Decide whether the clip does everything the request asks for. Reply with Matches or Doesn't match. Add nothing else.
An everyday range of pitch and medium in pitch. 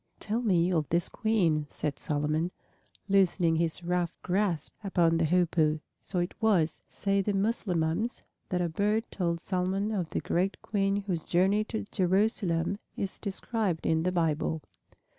Matches